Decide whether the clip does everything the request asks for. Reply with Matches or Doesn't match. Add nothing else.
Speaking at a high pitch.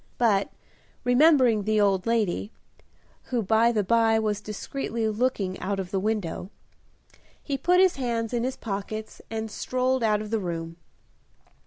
Matches